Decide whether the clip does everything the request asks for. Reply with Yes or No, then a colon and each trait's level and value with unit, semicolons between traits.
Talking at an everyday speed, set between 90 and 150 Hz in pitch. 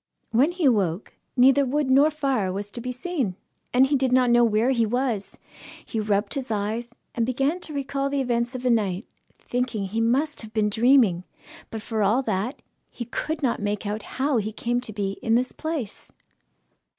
No: average, 195 wpm; high, 240 Hz